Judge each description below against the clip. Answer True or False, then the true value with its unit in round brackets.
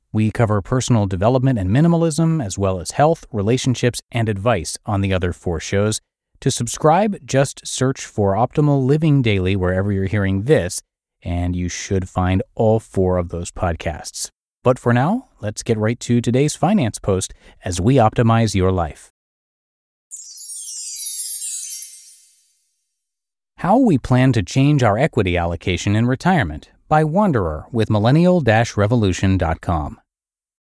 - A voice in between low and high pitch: False (110 Hz)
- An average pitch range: False (5.9 semitones)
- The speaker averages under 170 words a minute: True (135 wpm)